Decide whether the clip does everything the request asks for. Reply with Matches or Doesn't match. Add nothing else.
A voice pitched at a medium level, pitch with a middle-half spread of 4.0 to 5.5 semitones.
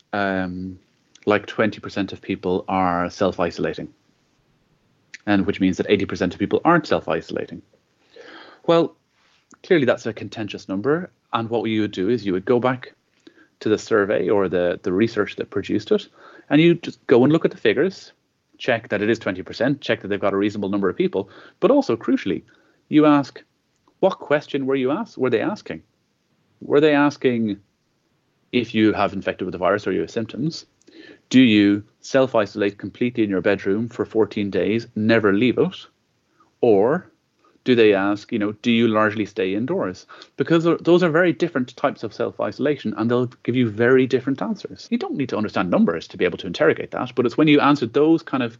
Doesn't match